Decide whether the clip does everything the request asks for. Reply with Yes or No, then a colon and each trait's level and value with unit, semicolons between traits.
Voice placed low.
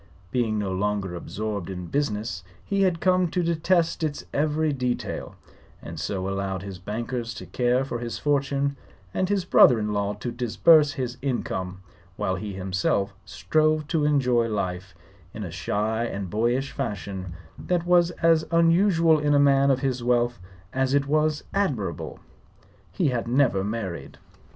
Yes: low, 125 Hz